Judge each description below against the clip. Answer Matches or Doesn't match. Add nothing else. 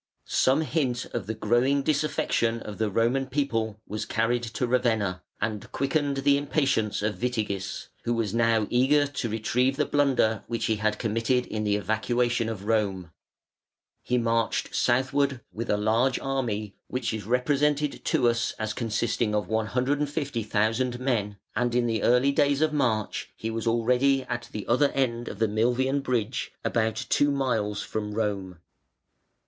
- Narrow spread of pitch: Doesn't match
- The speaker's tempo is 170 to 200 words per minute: Doesn't match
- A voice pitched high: Doesn't match